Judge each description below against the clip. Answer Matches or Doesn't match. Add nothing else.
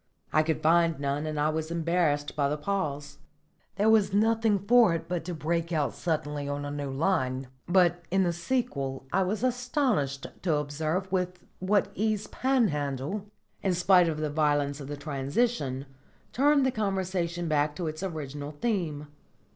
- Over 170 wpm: Doesn't match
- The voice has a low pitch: Doesn't match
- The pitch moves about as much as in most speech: Matches